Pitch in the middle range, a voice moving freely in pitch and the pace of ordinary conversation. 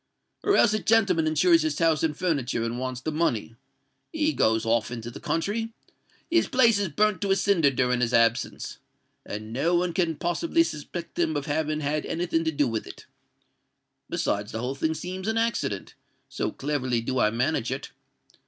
Yes: medium, 155 Hz; wide, 6.6 semitones; average, 180 wpm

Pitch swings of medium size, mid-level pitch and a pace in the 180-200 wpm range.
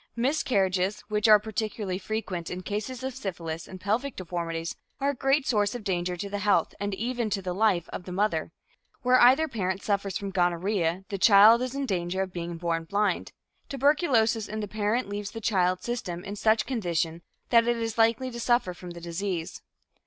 No: average, 4.2 semitones; high, 205 Hz; average, 190 wpm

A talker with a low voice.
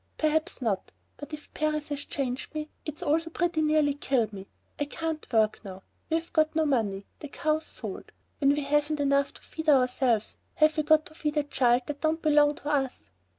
No: very high, 295 Hz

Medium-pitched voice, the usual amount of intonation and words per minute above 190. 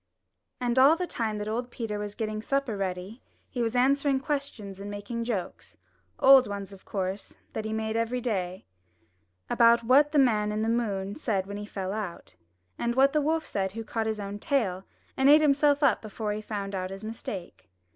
No: high, 220 Hz; average, 4.1 semitones; fast, 205 wpm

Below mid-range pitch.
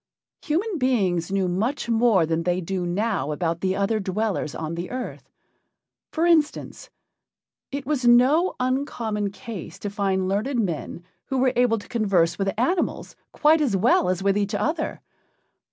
No: high, 210 Hz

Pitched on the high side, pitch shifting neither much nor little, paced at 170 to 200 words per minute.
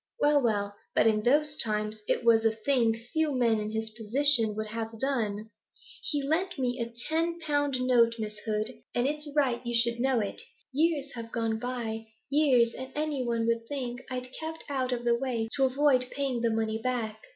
Yes: high, 240 Hz; average, 3.7 semitones; average, 195 wpm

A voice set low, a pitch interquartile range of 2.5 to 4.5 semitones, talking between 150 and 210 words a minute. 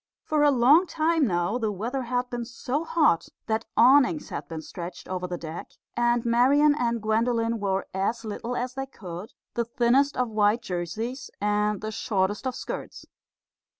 No: high, 235 Hz; average, 3.8 semitones; average, 170 wpm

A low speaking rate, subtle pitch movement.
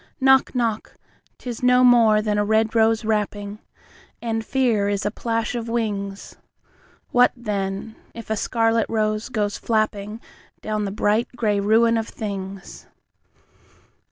Yes: slow, 125 wpm; narrow, 1.9 semitones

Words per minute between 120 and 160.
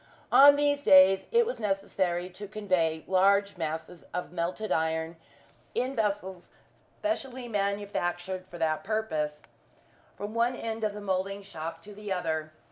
Yes: average, 140 wpm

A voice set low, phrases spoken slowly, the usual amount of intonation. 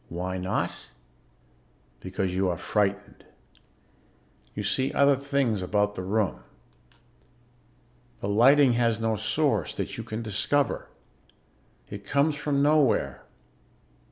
No: low, 110 Hz; slow, 110 wpm; wide, 6.1 semitones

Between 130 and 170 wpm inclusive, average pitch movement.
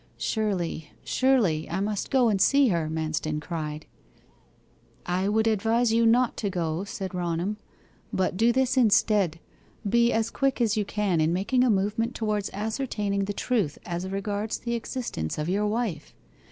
Yes: average, 160 wpm; average, 4.6 semitones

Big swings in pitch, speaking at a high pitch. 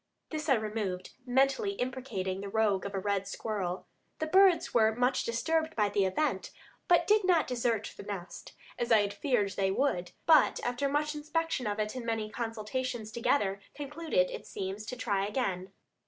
Yes: wide, 6.2 semitones; high, 230 Hz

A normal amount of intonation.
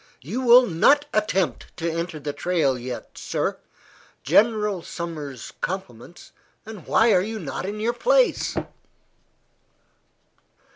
No: wide, 6.0 semitones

